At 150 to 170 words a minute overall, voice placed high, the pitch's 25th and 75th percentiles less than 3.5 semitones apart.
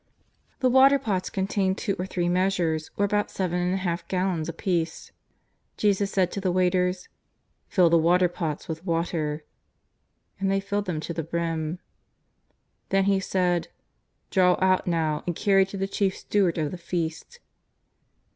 No: average, 165 wpm; medium, 180 Hz; narrow, 2.4 semitones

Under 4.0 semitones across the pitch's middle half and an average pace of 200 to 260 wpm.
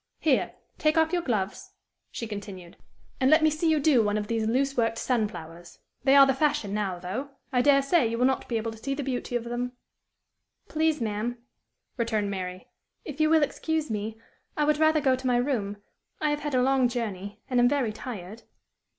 No: average, 5.2 semitones; fast, 205 wpm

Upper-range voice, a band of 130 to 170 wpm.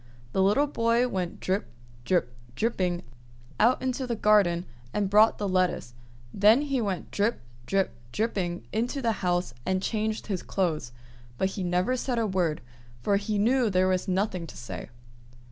Yes: high, 200 Hz; average, 160 wpm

